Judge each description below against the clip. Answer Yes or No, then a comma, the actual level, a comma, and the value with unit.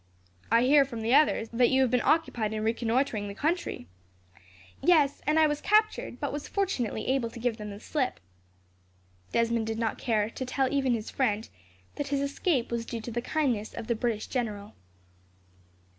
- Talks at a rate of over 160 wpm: Yes, average, 185 wpm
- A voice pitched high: Yes, high, 240 Hz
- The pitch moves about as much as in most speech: Yes, average, 3.9 semitones